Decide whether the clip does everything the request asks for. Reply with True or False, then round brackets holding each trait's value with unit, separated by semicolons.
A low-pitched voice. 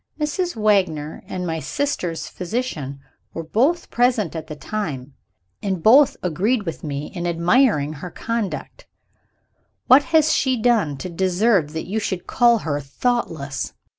False (190 Hz)